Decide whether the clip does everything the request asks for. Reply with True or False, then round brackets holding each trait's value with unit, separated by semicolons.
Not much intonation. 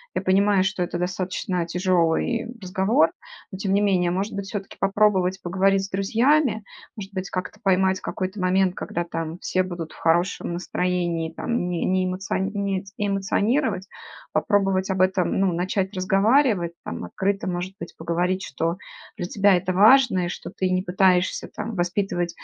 True (1.8 semitones)